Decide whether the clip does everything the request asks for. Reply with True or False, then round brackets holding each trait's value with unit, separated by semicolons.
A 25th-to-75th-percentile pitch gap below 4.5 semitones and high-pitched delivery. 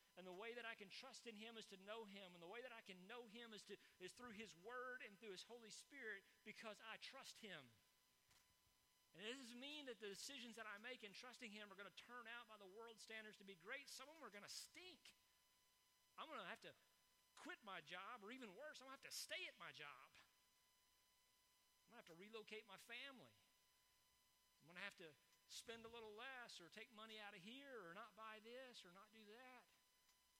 True (3.7 semitones; 220 Hz)